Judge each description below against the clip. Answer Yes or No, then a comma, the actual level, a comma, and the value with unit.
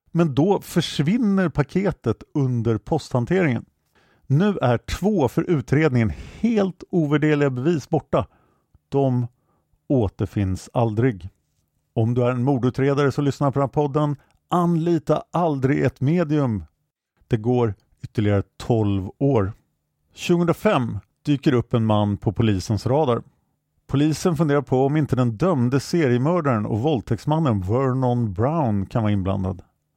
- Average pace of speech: No, slow, 120 wpm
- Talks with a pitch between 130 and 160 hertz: Yes, low, 135 Hz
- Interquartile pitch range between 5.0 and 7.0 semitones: Yes, wide, 5.4 semitones